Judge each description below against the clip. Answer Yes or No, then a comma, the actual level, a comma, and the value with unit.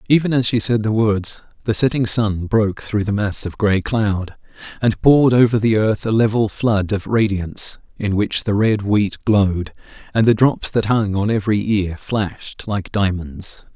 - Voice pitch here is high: No, low, 105 Hz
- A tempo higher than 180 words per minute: Yes, average, 190 wpm